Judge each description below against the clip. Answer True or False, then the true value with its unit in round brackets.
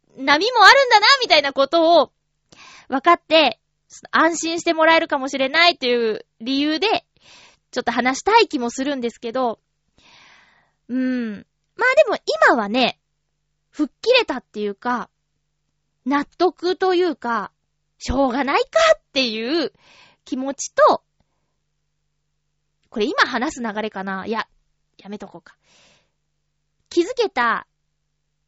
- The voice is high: True (255 Hz)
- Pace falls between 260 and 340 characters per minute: False (250 characters per minute)